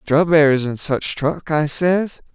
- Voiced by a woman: No, male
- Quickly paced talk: No, average, 155 wpm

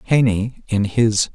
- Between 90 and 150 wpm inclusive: Yes, slow, 135 wpm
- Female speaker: No, male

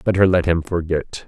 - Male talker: Yes, male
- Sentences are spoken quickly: No, average, 190 wpm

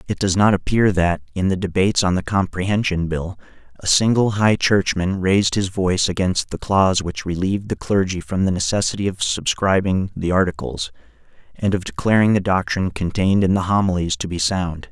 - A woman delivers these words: No, male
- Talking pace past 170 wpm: Yes, average, 180 wpm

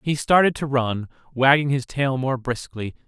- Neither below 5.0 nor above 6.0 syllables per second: No, 4.6 syllables/s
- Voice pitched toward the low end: Yes, low, 130 Hz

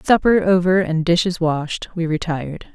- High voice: No, medium, 175 Hz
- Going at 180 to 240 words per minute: No, average, 155 wpm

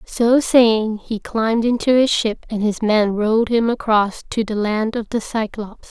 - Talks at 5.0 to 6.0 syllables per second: No, 4.4 syllables/s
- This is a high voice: Yes, high, 220 Hz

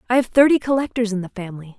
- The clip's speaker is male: No, female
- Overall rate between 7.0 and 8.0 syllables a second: Yes, 7.6 syllables/s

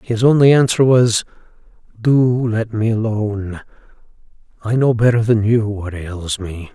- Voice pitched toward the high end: No, low, 110 Hz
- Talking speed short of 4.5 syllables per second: Yes, 4.2 syllables/s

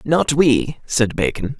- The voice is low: Yes, low, 130 Hz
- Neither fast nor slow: Yes, average, 150 wpm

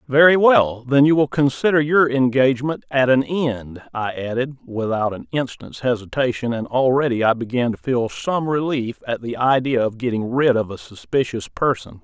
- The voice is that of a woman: No, male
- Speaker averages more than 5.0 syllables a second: No, 4.9 syllables/s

